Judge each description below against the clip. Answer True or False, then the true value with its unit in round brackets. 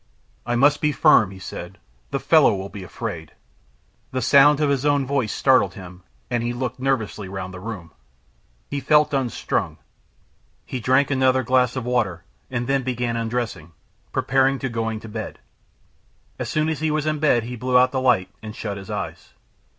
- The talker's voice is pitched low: True (125 Hz)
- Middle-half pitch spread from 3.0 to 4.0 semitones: True (3.7 semitones)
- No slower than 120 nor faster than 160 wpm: False (180 wpm)